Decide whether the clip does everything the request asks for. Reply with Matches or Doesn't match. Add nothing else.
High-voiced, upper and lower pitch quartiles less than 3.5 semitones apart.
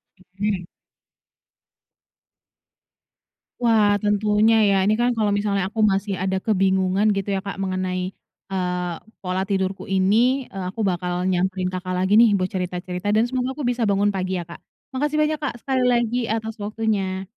Matches